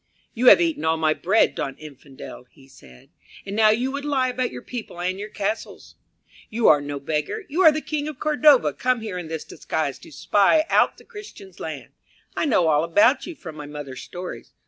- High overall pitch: Yes, high, 200 Hz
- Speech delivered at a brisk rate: Yes, fast, 210 wpm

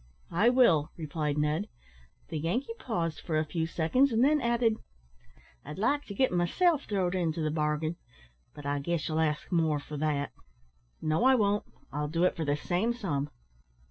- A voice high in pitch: No, medium, 165 Hz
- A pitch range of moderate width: No, wide, 6.4 semitones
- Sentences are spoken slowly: No, average, 175 wpm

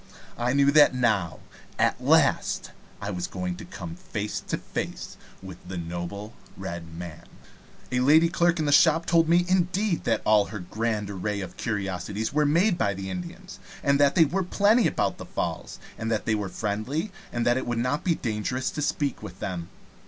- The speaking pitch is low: Yes, low, 115 Hz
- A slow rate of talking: No, average, 190 wpm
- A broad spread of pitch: Yes, wide, 8.0 semitones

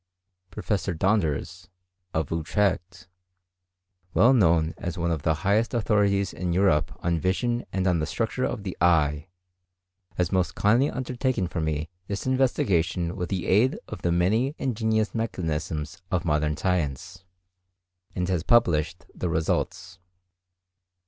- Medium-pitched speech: No, very low, 90 Hz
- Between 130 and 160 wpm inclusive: Yes, slow, 135 wpm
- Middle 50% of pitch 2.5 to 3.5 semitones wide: No, average, 3.9 semitones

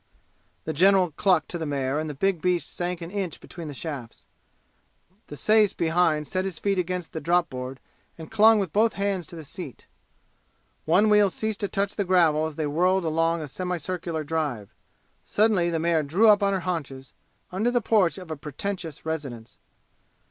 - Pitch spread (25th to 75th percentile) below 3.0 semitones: No, average, 3.9 semitones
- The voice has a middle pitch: Yes, medium, 170 Hz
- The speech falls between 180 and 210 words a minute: Yes, average, 185 wpm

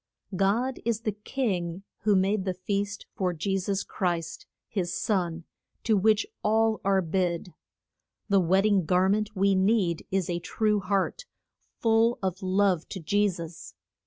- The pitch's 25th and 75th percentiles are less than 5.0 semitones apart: Yes, average, 2.7 semitones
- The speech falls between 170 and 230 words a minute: No, average, 155 wpm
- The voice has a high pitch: Yes, high, 195 Hz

